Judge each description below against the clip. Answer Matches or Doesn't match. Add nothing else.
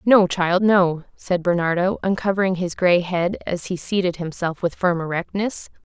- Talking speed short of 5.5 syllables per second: Matches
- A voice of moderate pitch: Matches